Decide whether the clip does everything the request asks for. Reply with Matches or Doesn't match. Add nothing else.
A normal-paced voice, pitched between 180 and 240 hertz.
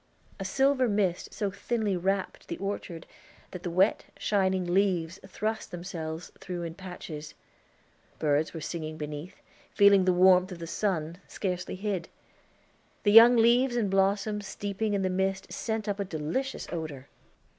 Matches